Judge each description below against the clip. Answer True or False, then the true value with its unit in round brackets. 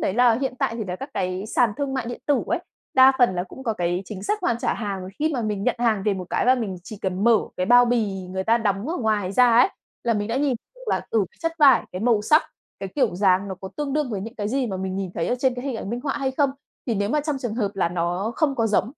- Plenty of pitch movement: False (5.0 semitones)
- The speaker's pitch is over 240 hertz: False (225 Hz)